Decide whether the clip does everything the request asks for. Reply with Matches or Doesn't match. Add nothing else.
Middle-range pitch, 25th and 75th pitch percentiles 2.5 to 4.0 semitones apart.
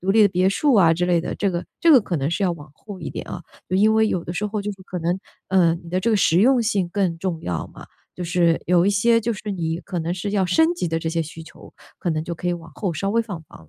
Matches